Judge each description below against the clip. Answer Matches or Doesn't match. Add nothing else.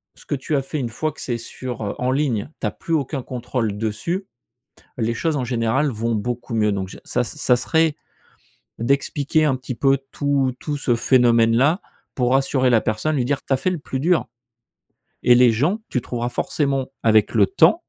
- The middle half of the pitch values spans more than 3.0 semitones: Matches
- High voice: Doesn't match